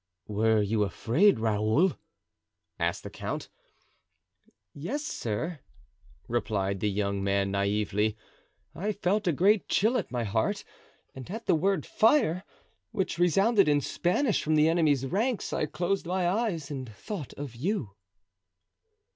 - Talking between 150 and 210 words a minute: No, slow, 135 wpm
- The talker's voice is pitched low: No, medium, 150 Hz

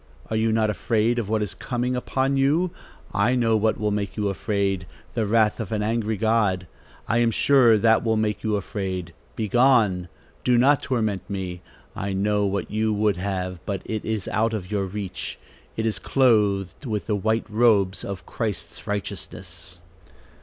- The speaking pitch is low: Yes, low, 105 Hz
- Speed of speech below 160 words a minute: No, average, 175 wpm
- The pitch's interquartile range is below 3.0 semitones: Yes, narrow, 2.4 semitones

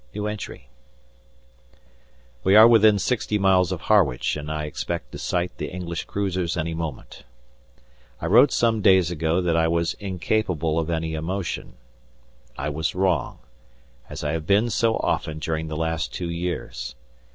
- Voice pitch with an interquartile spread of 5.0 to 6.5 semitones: No, average, 3.3 semitones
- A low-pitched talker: Yes, very low, 85 Hz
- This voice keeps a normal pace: Yes, average, 150 wpm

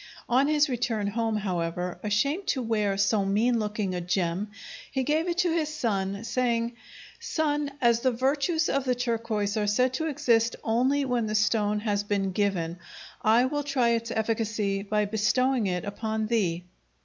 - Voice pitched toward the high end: Yes, high, 225 Hz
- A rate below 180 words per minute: Yes, average, 170 wpm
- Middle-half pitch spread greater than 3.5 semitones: Yes, average, 4.0 semitones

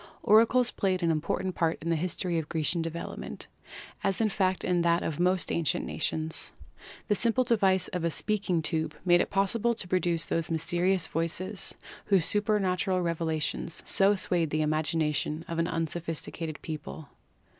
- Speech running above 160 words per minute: Yes, average, 175 wpm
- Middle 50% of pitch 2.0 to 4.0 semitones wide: Yes, average, 2.8 semitones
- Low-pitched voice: No, medium, 170 Hz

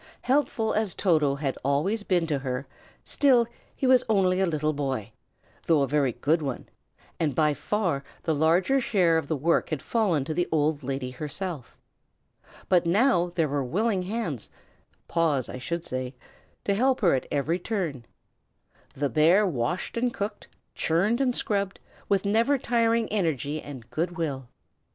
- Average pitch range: No, wide, 6.3 semitones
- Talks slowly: No, average, 160 wpm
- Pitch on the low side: No, medium, 165 Hz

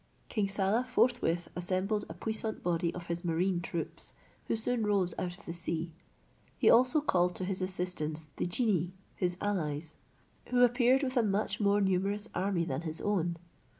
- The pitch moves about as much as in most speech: Yes, average, 3.8 semitones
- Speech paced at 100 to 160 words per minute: No, average, 170 wpm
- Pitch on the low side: No, medium, 185 Hz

